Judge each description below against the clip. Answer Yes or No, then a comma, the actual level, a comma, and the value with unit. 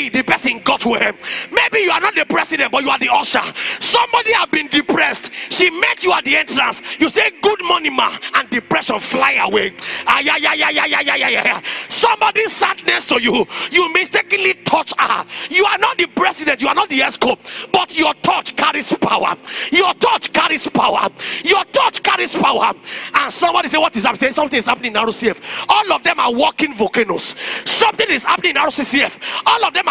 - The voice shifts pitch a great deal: Yes, wide, 5.9 semitones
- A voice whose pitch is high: Yes, very high, 355 Hz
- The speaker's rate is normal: Yes, average, 185 wpm